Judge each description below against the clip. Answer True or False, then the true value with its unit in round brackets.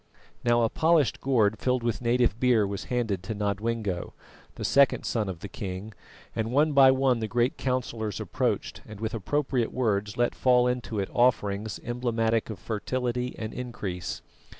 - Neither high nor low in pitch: False (115 Hz)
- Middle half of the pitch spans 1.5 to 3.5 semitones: True (3.1 semitones)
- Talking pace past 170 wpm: False (165 wpm)